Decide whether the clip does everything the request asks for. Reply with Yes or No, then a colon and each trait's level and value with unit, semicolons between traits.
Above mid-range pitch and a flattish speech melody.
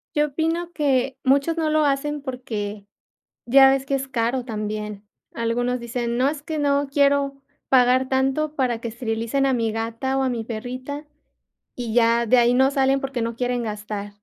No: very high, 255 Hz; average, 3.0 semitones